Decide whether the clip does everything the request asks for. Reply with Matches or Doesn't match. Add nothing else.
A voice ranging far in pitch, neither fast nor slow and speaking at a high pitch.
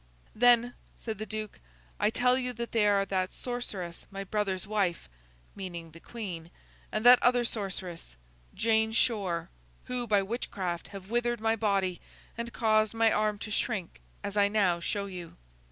Doesn't match